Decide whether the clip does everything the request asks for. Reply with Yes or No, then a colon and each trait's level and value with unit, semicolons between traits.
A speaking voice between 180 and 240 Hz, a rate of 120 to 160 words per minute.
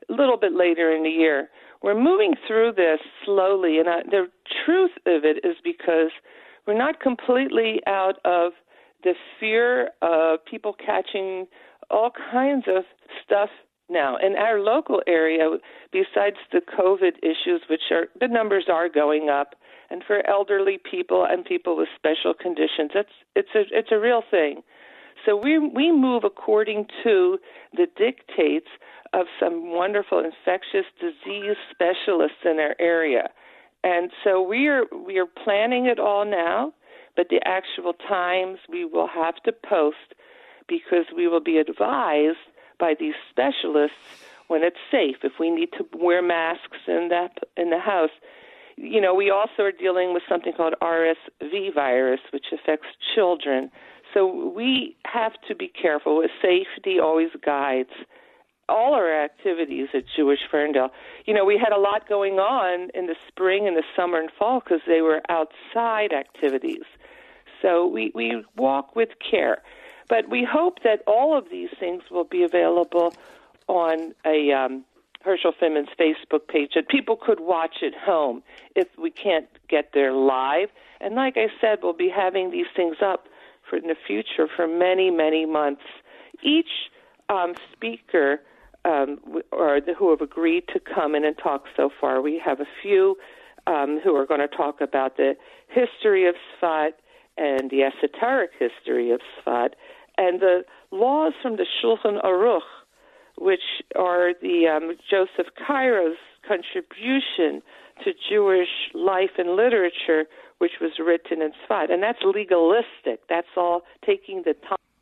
Yes: high, 190 Hz; average, 155 wpm